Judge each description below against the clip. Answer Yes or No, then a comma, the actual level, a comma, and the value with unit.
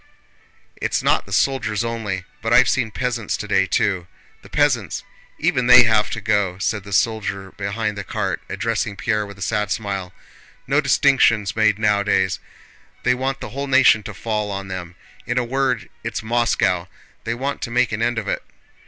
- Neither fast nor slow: Yes, average, 170 wpm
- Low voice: Yes, low, 110 Hz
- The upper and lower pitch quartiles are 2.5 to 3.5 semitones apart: Yes, average, 3.2 semitones